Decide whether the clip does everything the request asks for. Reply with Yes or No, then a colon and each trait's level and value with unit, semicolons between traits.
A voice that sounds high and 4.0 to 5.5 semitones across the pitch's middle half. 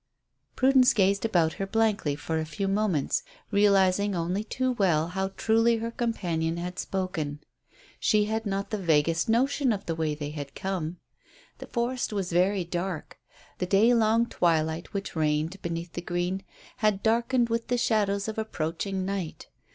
Yes: high, 195 Hz; average, 4.7 semitones